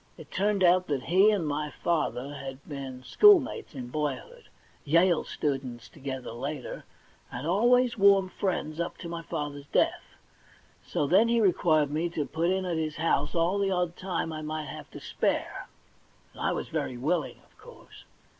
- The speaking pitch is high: No, medium, 165 Hz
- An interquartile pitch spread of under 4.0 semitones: No, average, 4.7 semitones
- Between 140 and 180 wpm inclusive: Yes, average, 175 wpm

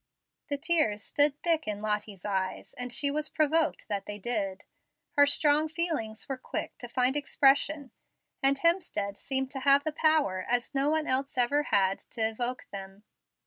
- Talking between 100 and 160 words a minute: No, average, 170 wpm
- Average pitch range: No, wide, 5.8 semitones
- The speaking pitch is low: No, very high, 265 Hz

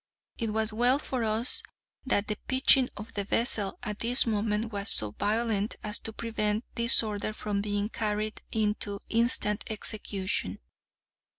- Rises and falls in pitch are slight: Yes, narrow, 1.8 semitones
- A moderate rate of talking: Yes, average, 150 wpm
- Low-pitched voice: No, high, 215 Hz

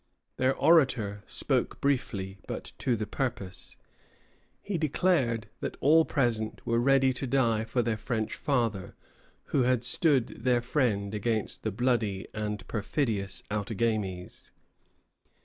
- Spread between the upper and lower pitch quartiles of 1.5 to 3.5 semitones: No, average, 3.9 semitones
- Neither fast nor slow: No, slow, 125 wpm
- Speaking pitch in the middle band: No, low, 115 Hz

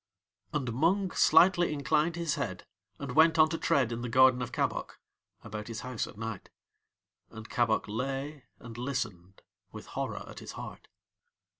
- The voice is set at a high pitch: No, low, 130 Hz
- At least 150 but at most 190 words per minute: Yes, average, 160 wpm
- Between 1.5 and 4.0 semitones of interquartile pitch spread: No, average, 5.2 semitones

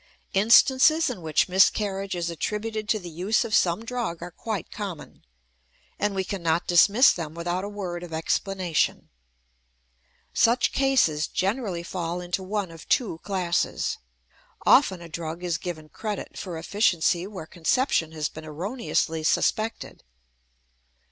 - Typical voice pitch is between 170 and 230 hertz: Yes, medium, 185 Hz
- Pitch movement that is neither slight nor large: Yes, average, 3.8 semitones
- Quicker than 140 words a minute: No, slow, 135 wpm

